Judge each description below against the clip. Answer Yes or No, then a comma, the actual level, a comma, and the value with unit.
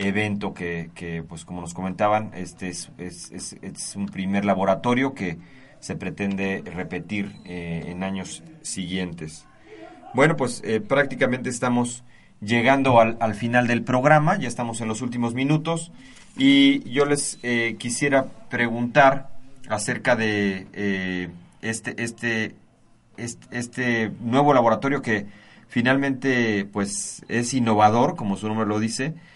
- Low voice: Yes, low, 115 Hz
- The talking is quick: No, average, 135 wpm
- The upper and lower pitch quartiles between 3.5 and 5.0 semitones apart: Yes, average, 4.3 semitones